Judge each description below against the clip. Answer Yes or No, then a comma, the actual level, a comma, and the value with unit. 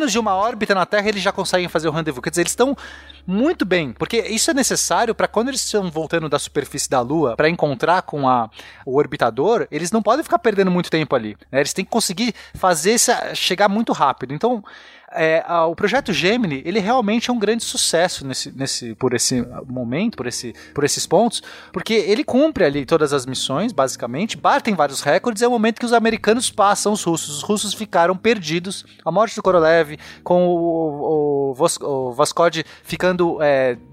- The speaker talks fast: Yes, fast, 195 wpm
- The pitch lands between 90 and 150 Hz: No, medium, 180 Hz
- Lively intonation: Yes, wide, 6.7 semitones